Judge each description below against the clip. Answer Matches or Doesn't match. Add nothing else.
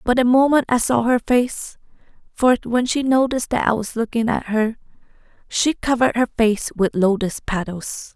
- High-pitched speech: Matches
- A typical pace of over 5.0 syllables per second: Doesn't match